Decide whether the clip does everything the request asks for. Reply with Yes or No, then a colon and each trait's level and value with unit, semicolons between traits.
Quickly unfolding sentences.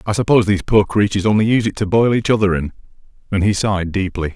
Yes: fast, 235 wpm